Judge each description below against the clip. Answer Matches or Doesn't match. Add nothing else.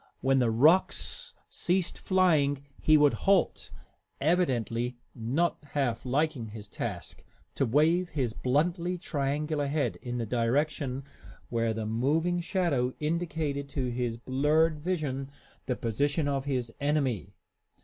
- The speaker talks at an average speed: Doesn't match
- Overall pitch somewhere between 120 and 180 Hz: Matches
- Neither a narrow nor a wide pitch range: Matches